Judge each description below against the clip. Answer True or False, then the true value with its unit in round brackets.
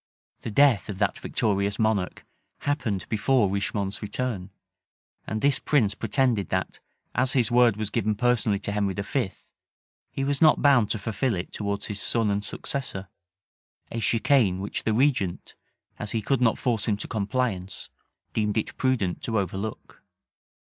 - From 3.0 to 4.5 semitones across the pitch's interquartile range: True (3.9 semitones)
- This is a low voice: True (110 Hz)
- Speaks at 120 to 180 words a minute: True (155 wpm)